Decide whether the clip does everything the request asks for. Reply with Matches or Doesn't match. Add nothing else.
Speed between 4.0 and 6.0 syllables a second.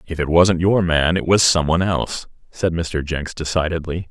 Matches